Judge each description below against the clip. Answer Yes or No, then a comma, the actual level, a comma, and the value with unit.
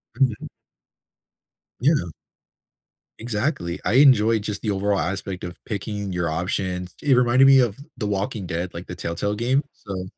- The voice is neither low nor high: No, low, 105 Hz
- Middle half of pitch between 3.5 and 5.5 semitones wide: Yes, average, 4.7 semitones